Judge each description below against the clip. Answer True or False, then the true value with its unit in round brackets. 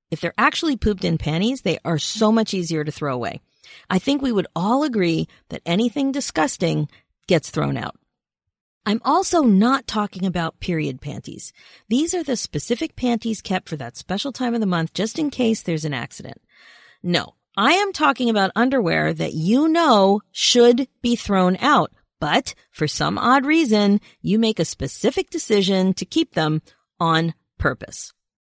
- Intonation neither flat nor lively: False (7.2 semitones)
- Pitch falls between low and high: False (210 Hz)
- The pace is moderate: True (170 wpm)